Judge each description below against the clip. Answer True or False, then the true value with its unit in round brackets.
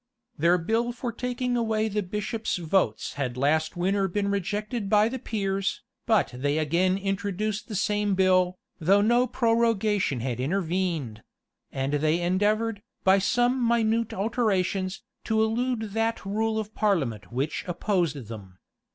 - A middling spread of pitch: True (4.2 semitones)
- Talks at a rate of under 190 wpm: True (140 wpm)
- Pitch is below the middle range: False (200 Hz)